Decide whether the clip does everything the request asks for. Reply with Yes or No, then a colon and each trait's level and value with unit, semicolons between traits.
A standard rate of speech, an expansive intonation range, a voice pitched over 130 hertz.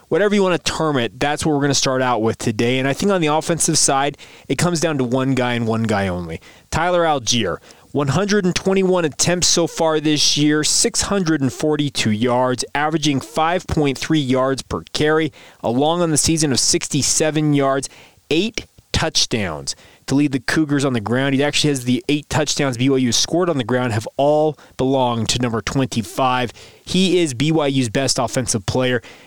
No: average, 175 wpm; average, 3.9 semitones; medium, 140 Hz